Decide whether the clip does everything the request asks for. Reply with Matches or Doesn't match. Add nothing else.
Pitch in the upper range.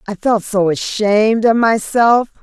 Matches